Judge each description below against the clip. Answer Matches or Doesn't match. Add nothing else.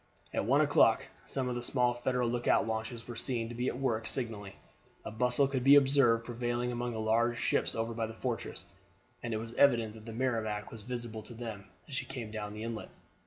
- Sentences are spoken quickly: Matches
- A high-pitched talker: Doesn't match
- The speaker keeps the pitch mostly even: Matches